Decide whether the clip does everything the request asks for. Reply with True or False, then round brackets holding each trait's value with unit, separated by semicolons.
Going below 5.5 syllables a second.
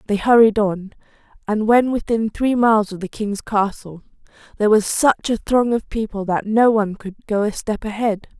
True (5.0 syllables/s)